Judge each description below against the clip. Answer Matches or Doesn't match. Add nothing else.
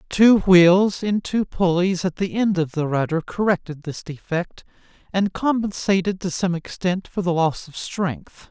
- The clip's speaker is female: Doesn't match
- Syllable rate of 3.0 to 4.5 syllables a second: Matches